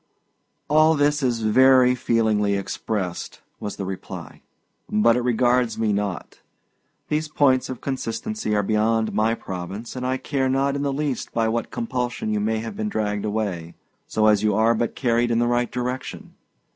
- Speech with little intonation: No, average, 3.4 semitones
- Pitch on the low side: Yes, low, 115 Hz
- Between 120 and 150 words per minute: No, average, 170 wpm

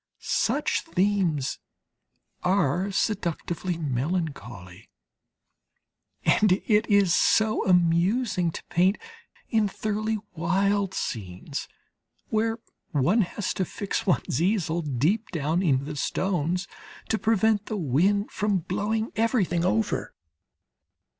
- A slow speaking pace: Yes, slow, 100 wpm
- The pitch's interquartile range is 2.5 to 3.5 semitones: No, average, 4.5 semitones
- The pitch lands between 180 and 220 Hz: Yes, medium, 185 Hz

